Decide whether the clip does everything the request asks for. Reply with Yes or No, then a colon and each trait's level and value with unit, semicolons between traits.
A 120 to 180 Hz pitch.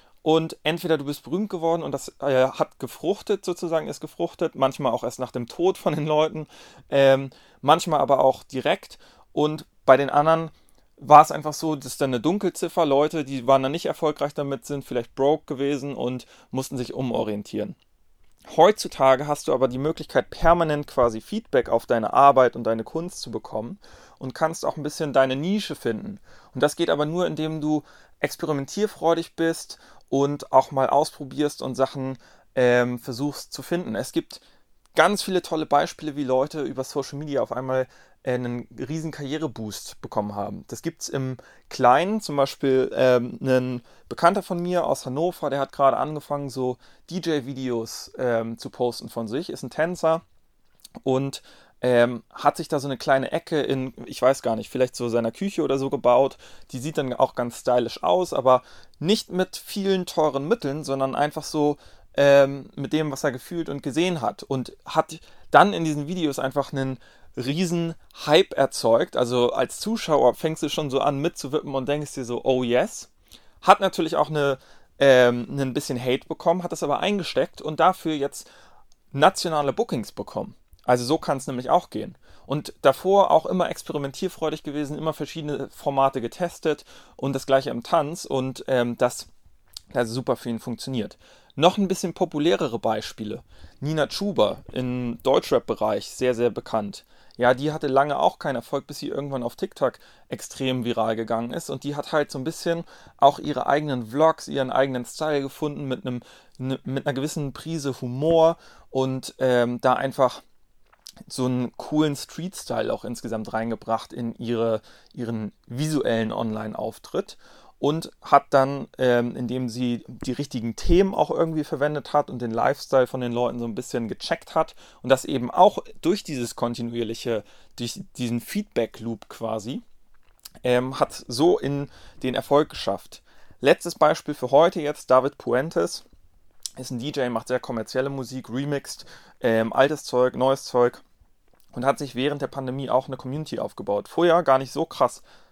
Yes: medium, 140 Hz